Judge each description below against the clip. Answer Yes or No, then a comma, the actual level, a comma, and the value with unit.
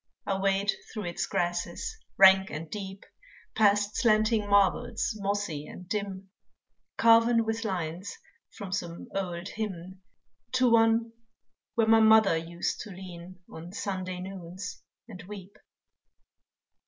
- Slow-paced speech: Yes, slow, 120 wpm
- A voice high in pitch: Yes, high, 195 Hz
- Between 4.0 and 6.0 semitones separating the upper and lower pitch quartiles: No, average, 3.1 semitones